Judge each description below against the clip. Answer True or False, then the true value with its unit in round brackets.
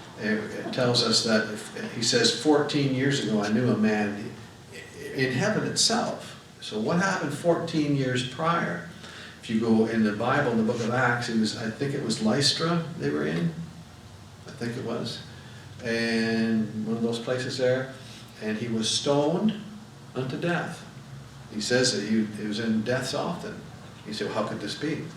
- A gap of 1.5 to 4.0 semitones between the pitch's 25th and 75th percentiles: False (4.5 semitones)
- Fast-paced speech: False (180 wpm)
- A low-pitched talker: True (120 Hz)